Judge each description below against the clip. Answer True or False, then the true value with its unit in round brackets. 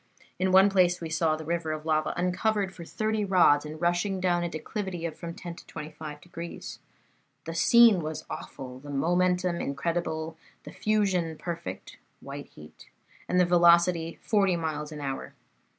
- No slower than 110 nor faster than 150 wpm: False (165 wpm)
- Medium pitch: True (170 Hz)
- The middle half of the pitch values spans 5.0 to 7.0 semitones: False (2.7 semitones)